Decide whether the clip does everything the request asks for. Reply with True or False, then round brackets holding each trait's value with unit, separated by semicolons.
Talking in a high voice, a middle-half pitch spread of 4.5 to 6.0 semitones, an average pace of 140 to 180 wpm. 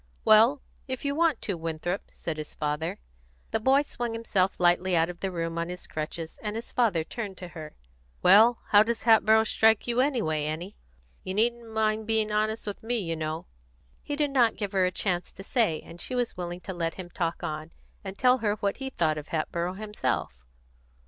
False (200 Hz; 5.1 semitones; 200 wpm)